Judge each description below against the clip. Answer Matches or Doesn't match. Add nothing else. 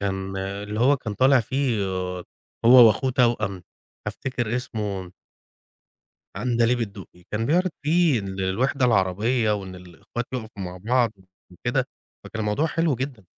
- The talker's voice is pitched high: Doesn't match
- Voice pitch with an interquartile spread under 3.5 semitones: Doesn't match